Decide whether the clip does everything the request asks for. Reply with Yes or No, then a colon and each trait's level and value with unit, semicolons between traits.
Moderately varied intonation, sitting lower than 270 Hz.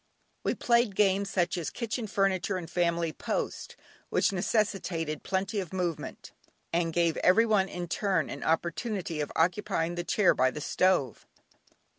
Yes: average, 3.1 semitones; medium, 185 Hz